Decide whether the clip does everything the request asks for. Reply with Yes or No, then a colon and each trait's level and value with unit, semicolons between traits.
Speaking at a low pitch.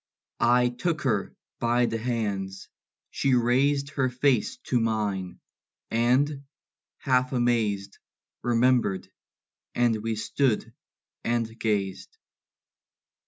Yes: low, 120 Hz